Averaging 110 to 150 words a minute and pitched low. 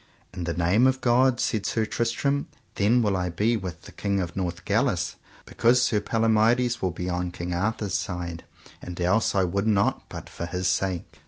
No: average, 185 wpm; low, 100 Hz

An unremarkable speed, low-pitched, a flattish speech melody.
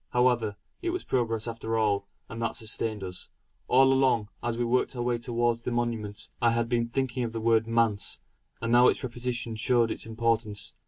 Yes: average, 195 wpm; low, 115 Hz; narrow, 1.4 semitones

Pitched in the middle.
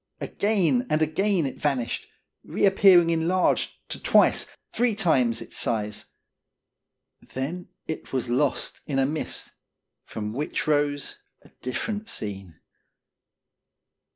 Yes: medium, 150 Hz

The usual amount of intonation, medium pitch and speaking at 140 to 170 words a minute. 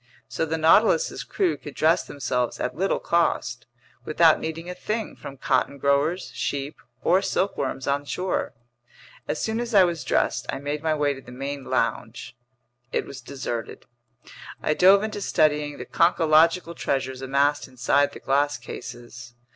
Yes: average, 4.1 semitones; medium, 145 Hz; average, 155 wpm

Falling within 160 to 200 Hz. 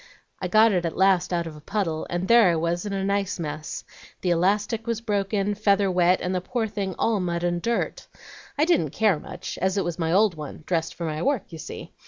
Yes: medium, 185 Hz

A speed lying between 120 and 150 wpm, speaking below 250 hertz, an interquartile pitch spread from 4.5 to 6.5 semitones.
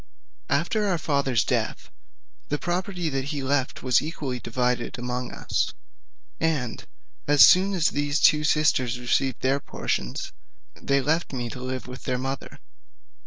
No: average, 145 wpm; medium, 140 Hz; average, 3.4 semitones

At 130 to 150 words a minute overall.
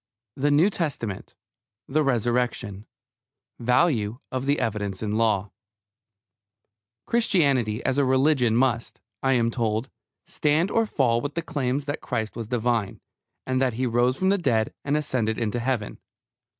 Yes: average, 145 wpm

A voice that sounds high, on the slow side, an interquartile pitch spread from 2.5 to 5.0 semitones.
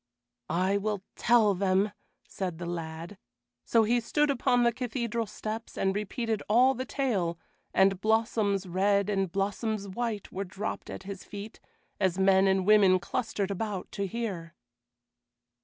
No: high, 200 Hz; average, 145 wpm; average, 2.8 semitones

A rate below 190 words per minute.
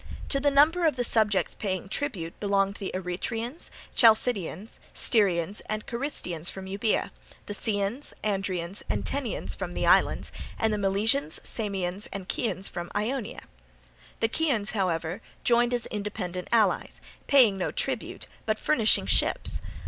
Yes: average, 140 wpm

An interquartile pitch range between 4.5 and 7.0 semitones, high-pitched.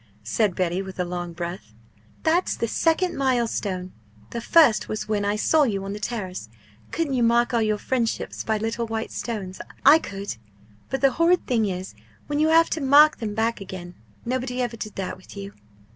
Yes: average, 5.2 semitones; high, 225 Hz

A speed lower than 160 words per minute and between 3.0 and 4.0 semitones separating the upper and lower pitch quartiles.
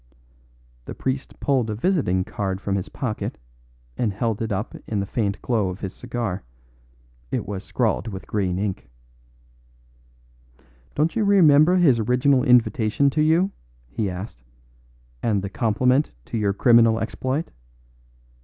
No: average, 140 wpm; average, 5.0 semitones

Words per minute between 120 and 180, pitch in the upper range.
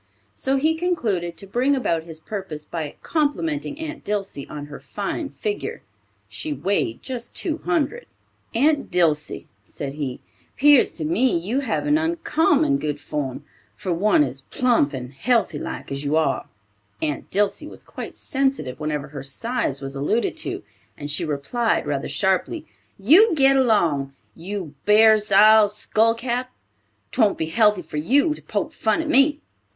Yes: average, 155 wpm; high, 205 Hz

